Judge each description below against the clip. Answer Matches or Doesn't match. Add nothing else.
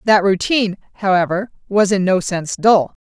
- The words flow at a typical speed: Matches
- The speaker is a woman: Matches